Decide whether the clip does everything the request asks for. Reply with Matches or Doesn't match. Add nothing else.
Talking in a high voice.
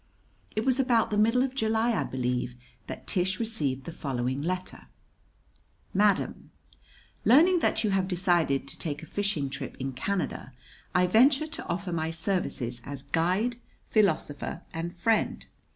Doesn't match